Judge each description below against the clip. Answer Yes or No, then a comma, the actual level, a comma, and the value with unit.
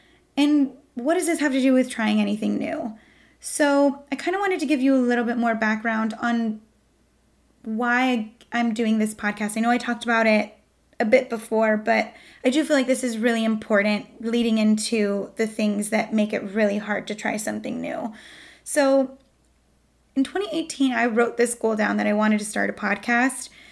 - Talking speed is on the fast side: No, average, 190 wpm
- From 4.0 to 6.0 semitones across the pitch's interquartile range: No, average, 3.4 semitones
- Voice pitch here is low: No, high, 235 Hz